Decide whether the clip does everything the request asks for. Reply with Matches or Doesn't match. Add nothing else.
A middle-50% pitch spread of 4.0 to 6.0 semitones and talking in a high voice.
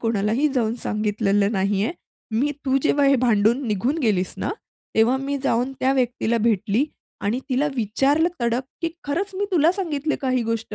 Matches